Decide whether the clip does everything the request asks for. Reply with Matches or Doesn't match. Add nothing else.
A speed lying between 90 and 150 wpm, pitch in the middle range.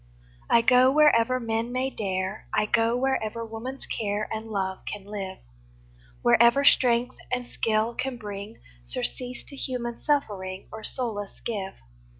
Doesn't match